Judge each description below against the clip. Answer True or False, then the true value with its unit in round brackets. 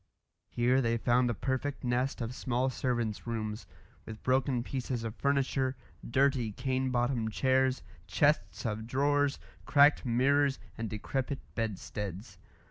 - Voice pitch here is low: True (125 Hz)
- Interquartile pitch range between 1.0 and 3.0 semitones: True (2.7 semitones)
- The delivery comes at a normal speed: False (130 wpm)